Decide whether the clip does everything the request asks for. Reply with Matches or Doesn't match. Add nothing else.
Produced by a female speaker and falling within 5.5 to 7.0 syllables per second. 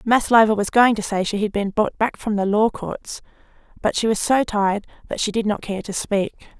Doesn't match